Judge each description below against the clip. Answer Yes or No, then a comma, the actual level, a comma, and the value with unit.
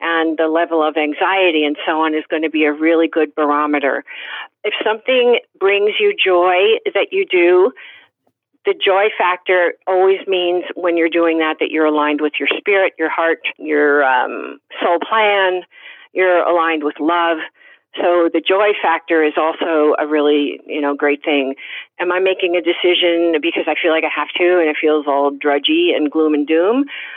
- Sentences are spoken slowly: No, average, 180 wpm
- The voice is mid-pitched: Yes, medium, 165 Hz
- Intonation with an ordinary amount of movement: Yes, average, 3.5 semitones